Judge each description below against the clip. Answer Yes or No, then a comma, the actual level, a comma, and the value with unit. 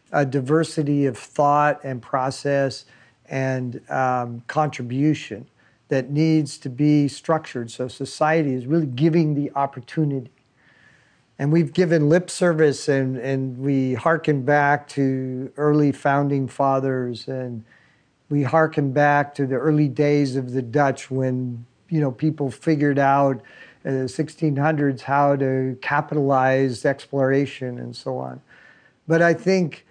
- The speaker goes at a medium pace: No, slow, 130 wpm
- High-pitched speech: No, medium, 140 Hz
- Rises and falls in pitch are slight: Yes, narrow, 2.3 semitones